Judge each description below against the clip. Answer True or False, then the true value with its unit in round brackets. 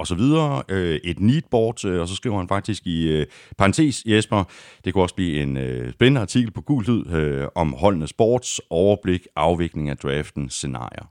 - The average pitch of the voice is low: True (95 Hz)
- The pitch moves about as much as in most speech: False (6.6 semitones)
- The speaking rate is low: False (185 wpm)